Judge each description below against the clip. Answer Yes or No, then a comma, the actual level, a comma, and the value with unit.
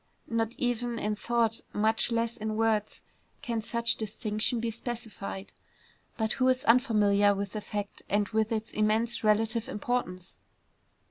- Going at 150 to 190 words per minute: No, average, 140 wpm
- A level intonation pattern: Yes, narrow, 1.9 semitones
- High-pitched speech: Yes, high, 220 Hz